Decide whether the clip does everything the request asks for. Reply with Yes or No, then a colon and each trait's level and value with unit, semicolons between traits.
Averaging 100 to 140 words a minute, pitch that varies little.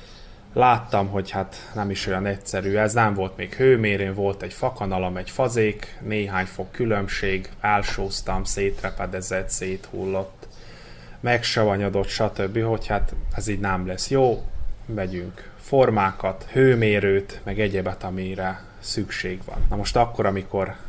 Yes: average, 125 wpm; narrow, 2.2 semitones